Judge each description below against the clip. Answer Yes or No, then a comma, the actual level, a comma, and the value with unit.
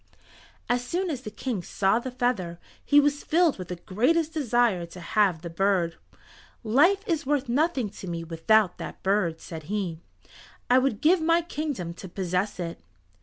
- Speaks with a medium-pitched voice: No, high, 215 Hz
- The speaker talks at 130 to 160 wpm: No, average, 170 wpm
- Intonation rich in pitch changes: Yes, wide, 8.2 semitones